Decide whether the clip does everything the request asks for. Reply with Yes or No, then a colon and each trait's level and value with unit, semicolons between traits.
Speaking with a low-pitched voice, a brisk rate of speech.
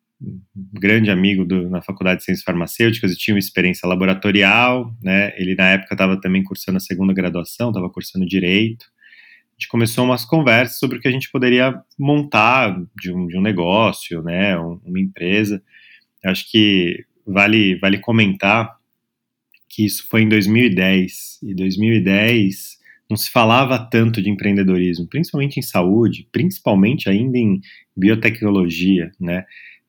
No: low, 100 Hz; average, 150 wpm